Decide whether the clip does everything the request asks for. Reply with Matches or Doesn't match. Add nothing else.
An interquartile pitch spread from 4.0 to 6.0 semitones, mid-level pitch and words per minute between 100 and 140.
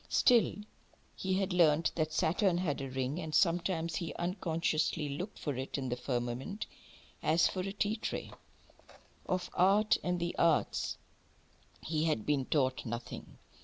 Doesn't match